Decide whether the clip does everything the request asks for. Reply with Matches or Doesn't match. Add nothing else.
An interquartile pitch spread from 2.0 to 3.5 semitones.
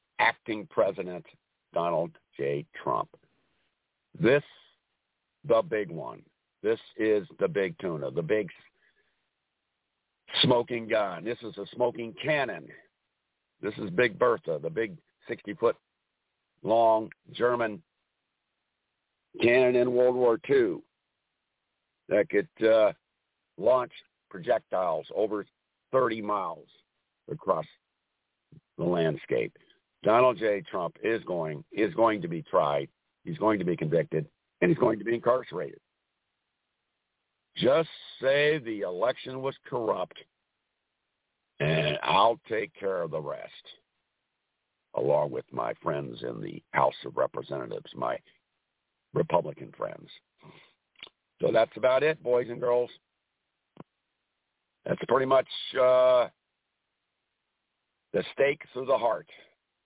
Doesn't match